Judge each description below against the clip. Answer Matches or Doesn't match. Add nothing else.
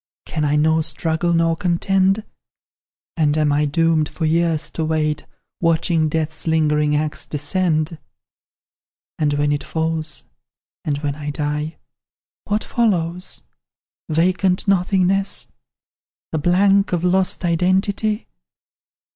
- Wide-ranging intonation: Doesn't match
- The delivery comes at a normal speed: Doesn't match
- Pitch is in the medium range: Matches